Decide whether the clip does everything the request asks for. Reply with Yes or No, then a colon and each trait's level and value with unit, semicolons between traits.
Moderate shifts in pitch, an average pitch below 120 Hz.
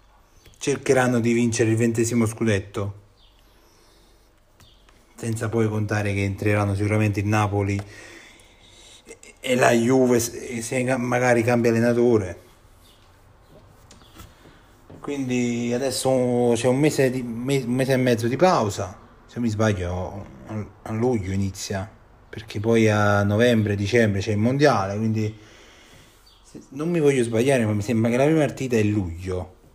Yes: average, 3.1 semitones; low, 110 Hz